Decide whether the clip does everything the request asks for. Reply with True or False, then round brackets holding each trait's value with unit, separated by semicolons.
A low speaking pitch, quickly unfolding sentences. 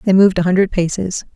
False (185 Hz; 220 wpm)